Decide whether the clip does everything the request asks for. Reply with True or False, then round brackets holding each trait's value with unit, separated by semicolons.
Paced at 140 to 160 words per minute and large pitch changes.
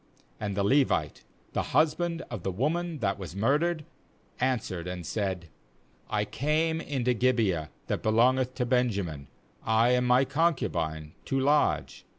True (150 wpm; 6.9 semitones)